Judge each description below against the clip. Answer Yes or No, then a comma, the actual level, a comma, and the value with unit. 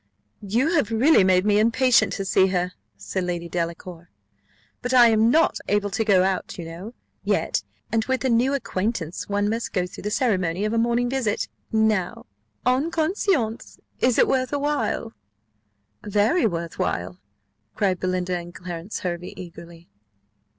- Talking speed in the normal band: Yes, average, 160 wpm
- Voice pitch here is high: Yes, high, 205 Hz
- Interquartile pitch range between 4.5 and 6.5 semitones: Yes, average, 5.0 semitones